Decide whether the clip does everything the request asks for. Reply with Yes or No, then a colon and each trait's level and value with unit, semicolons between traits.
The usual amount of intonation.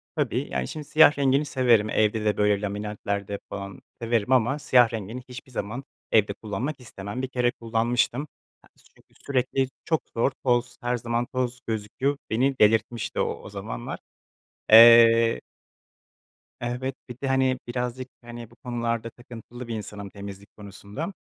Yes: average, 3.2 semitones